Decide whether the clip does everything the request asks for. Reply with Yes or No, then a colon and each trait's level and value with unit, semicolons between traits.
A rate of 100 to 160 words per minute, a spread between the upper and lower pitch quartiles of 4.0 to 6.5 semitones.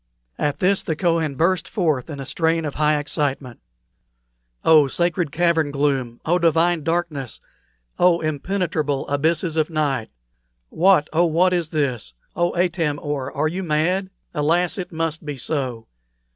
No: average, 145 wpm; average, 3.1 semitones